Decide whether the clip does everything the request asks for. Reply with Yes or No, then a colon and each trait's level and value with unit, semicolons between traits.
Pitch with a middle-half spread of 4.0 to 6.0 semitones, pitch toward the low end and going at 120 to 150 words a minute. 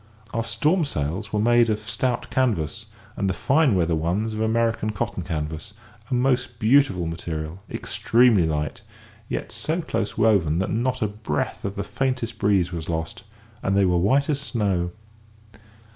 No: wide, 5.6 semitones; low, 105 Hz; average, 160 wpm